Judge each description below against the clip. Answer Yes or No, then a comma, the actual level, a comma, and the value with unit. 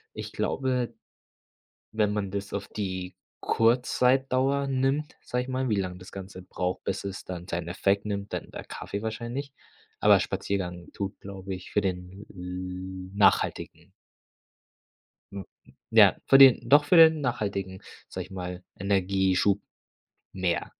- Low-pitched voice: Yes, low, 100 Hz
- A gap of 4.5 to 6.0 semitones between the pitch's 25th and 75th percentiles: Yes, average, 5.0 semitones